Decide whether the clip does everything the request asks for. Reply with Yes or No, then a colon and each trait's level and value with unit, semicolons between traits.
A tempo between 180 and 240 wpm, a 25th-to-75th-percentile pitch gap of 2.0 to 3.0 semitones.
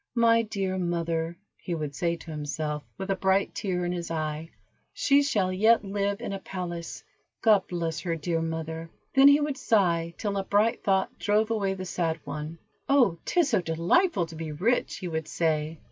No: average, 190 wpm; average, 4.0 semitones